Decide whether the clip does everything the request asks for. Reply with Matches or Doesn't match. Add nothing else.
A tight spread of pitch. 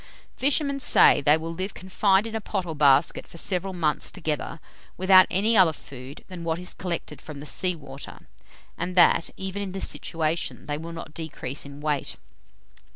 Doesn't match